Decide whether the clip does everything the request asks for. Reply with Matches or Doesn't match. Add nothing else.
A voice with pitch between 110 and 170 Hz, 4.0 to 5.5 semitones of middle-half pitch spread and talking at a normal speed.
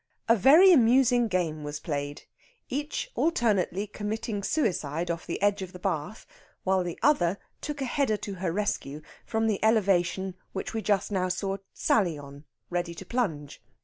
Doesn't match